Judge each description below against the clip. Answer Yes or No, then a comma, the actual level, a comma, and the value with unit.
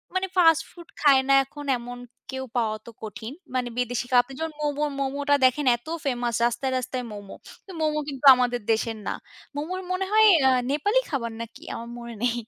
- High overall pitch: Yes, very high, 265 Hz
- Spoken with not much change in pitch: No, average, 3.8 semitones